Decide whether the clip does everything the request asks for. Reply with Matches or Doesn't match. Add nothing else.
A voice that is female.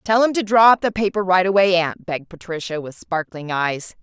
Matches